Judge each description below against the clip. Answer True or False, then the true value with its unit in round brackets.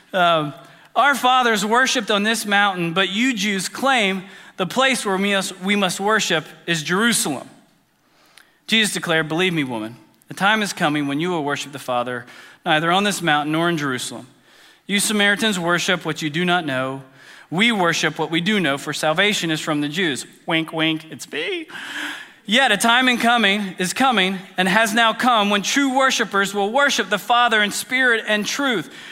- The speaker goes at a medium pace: True (180 wpm)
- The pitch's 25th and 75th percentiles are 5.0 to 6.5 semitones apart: True (5.5 semitones)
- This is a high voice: True (195 Hz)